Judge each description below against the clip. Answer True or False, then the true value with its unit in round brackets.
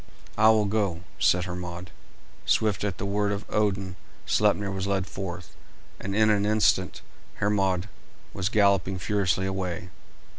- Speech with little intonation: True (2.0 semitones)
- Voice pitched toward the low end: True (100 Hz)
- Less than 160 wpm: True (140 wpm)